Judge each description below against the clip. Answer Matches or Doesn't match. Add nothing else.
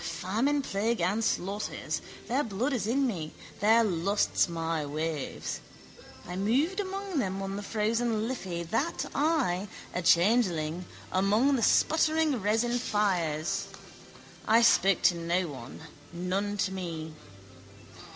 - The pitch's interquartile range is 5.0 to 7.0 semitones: Matches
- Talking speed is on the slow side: Matches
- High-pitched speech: Matches